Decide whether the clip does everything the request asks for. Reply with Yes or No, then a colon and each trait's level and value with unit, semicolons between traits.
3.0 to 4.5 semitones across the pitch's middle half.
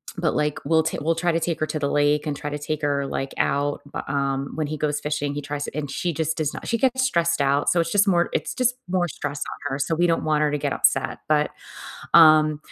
No: narrow, 2.4 semitones